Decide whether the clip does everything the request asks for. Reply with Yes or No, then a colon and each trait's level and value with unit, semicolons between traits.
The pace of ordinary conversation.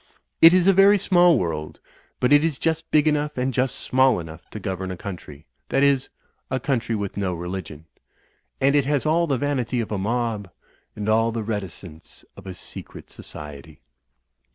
Yes: average, 190 wpm